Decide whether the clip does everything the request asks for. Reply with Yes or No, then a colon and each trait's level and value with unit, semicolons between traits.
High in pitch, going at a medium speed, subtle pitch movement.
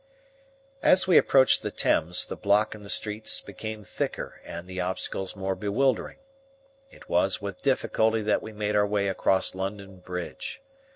No: low, 100 Hz; average, 160 wpm; narrow, 2.3 semitones